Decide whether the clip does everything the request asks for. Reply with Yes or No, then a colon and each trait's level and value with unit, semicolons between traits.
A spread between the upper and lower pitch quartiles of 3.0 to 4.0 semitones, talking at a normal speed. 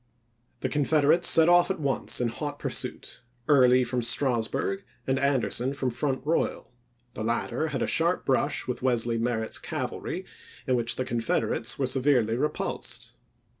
Yes: average, 3.5 semitones; average, 165 wpm